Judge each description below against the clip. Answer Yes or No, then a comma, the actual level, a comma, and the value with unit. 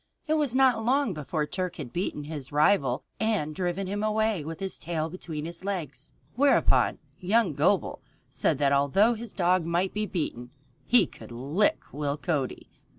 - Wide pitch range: Yes, wide, 6.1 semitones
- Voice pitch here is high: No, medium, 180 Hz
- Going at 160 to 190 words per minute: Yes, average, 165 wpm